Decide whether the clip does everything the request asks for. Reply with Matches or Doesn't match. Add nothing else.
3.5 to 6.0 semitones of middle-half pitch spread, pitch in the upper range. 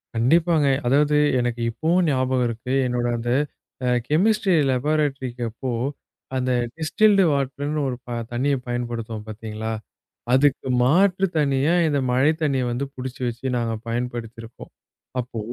Doesn't match